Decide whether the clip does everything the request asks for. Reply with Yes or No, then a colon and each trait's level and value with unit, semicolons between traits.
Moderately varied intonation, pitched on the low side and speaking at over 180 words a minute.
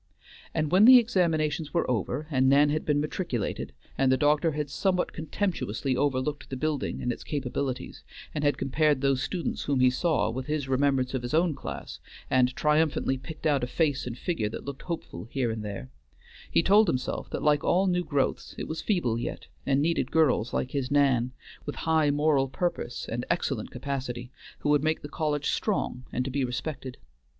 No: average, 3.5 semitones; medium, 145 Hz; average, 190 wpm